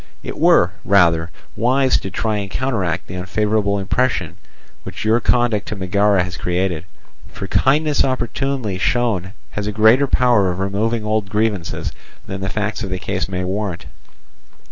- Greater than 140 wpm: Yes, average, 155 wpm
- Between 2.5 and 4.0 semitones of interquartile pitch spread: Yes, average, 3.7 semitones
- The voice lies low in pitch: Yes, low, 105 Hz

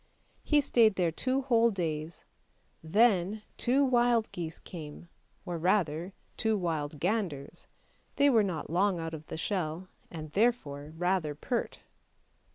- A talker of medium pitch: Yes, medium, 180 Hz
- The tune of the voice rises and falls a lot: Yes, wide, 5.9 semitones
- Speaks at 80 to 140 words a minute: Yes, slow, 135 wpm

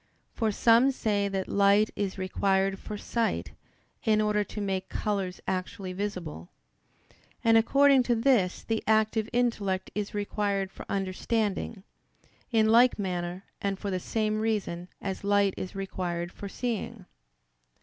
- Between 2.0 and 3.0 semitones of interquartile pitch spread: Yes, narrow, 2.5 semitones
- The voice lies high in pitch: Yes, high, 205 Hz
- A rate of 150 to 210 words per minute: No, average, 140 wpm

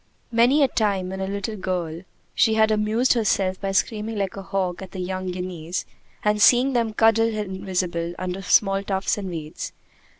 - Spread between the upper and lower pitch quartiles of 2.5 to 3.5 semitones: Yes, average, 2.8 semitones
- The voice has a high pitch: Yes, high, 195 Hz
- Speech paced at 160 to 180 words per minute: Yes, average, 175 wpm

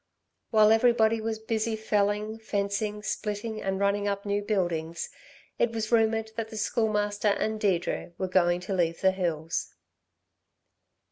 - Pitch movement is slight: Yes, narrow, 2.2 semitones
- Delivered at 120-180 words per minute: Yes, average, 140 wpm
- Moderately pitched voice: No, high, 210 Hz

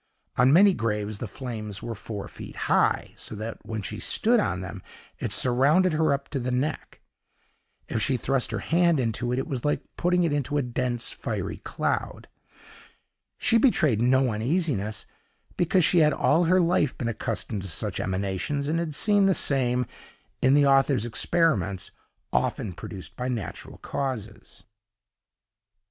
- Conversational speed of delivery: Yes, average, 160 wpm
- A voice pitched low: Yes, low, 130 Hz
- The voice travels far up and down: Yes, wide, 6.0 semitones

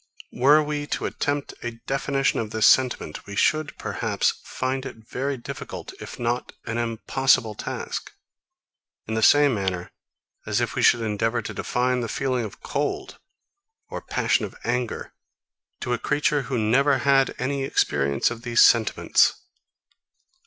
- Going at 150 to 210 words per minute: Yes, average, 155 wpm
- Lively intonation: No, average, 3.4 semitones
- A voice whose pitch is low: Yes, low, 125 Hz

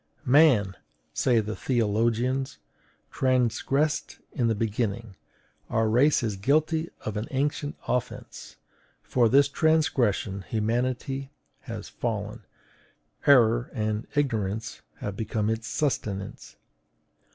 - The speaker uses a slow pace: Yes, slow, 100 wpm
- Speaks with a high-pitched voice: No, low, 120 Hz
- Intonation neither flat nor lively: Yes, average, 3.9 semitones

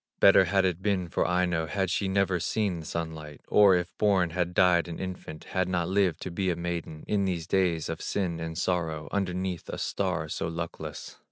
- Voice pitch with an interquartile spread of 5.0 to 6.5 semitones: No, narrow, 2.4 semitones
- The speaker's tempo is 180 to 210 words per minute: Yes, average, 200 wpm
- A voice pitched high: No, very low, 90 Hz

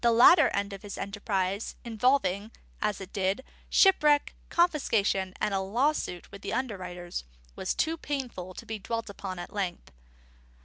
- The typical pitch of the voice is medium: No, high, 205 Hz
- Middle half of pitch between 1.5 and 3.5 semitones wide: No, average, 5.0 semitones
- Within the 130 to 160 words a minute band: Yes, average, 150 wpm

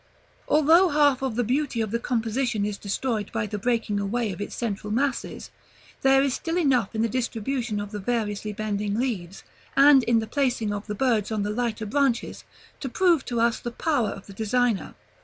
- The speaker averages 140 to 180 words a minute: No, average, 195 wpm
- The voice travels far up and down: No, average, 4.1 semitones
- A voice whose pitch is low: No, high, 230 Hz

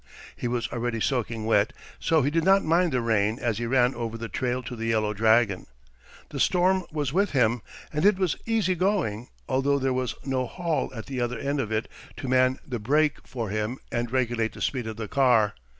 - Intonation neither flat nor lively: Yes, average, 4.1 semitones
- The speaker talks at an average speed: No, fast, 215 wpm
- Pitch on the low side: Yes, low, 125 Hz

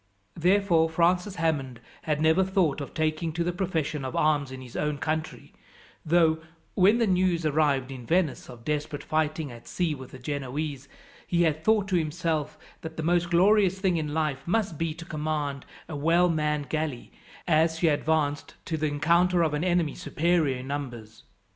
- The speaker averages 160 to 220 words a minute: Yes, average, 180 wpm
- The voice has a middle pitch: Yes, medium, 160 Hz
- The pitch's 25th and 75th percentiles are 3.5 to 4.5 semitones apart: No, average, 2.9 semitones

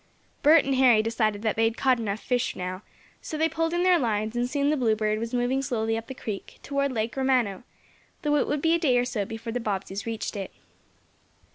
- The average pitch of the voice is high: Yes, high, 240 Hz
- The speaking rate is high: Yes, fast, 225 wpm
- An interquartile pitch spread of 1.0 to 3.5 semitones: No, average, 4.1 semitones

